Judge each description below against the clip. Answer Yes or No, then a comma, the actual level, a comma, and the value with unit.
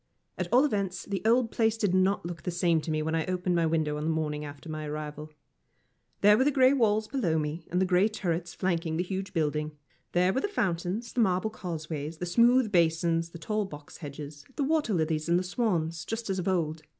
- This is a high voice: No, medium, 175 Hz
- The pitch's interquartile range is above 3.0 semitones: Yes, average, 4.7 semitones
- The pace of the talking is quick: Yes, fast, 220 wpm